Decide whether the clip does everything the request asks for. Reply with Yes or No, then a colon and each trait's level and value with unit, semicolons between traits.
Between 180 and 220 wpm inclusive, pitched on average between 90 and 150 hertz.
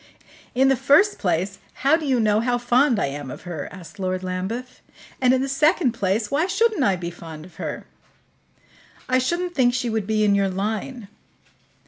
No: average, 190 wpm; high, 230 Hz